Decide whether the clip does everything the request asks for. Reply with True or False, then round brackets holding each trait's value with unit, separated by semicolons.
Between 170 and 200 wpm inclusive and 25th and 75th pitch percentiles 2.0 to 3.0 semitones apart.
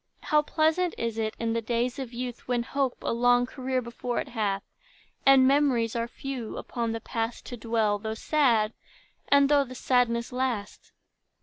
True (175 wpm; 2.5 semitones)